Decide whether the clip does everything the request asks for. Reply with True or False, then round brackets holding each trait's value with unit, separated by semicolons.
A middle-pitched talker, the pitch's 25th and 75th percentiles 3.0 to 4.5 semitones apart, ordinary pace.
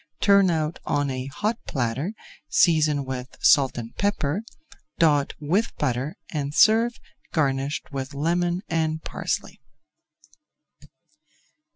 False (150 Hz; 4.1 semitones; 105 wpm)